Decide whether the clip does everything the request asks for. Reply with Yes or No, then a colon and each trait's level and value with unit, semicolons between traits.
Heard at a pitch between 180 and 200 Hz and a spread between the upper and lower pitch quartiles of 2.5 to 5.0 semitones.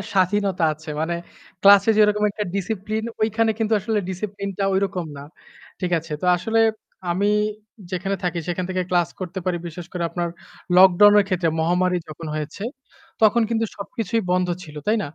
Yes: medium, 185 Hz; average, 2.9 semitones